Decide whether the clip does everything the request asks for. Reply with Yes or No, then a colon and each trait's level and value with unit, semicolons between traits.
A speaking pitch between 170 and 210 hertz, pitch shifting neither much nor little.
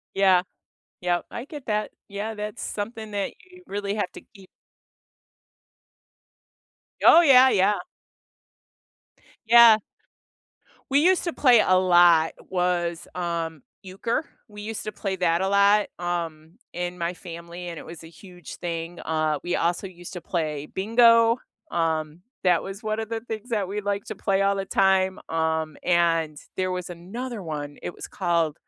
Yes: medium, 185 Hz; average, 3.7 semitones